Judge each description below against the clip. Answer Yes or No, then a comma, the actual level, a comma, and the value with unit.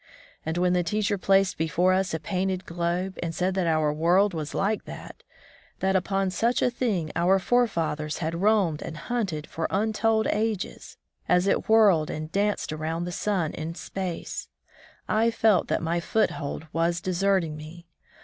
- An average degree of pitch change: Yes, average, 3.4 semitones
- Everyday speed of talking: Yes, average, 170 wpm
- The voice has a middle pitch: Yes, medium, 180 Hz